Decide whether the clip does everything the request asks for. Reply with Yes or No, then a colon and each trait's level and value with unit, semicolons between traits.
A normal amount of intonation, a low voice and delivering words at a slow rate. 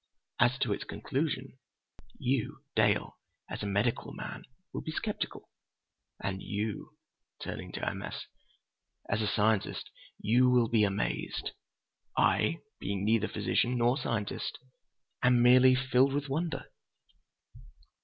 Yes: average, 3.9 semitones; low, 120 Hz; slow, 115 wpm